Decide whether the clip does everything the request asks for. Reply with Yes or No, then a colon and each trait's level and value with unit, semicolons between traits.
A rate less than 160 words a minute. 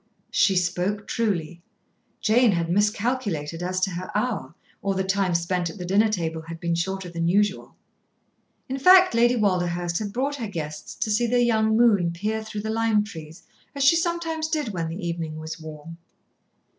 No: average, 180 wpm